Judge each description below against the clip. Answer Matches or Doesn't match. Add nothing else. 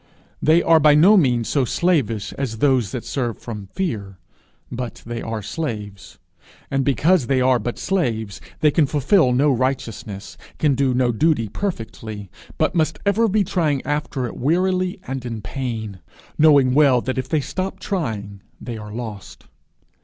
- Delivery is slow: Doesn't match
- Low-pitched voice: Matches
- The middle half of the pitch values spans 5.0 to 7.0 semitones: Matches